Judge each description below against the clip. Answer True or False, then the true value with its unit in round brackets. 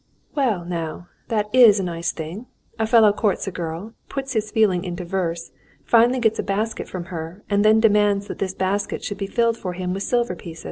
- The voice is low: False (200 Hz)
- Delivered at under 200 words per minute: False (205 wpm)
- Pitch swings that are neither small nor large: True (3.8 semitones)